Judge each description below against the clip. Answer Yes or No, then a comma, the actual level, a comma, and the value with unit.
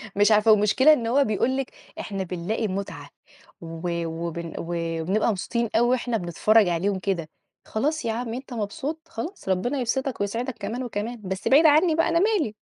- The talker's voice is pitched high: Yes, high, 220 Hz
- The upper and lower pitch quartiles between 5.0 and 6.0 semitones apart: Yes, wide, 5.4 semitones